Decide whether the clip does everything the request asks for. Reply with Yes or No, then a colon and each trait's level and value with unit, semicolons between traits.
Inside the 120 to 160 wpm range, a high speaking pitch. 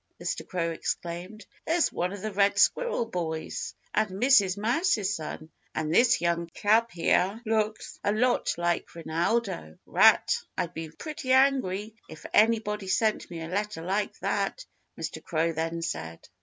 Yes: average, 150 wpm; high, 200 Hz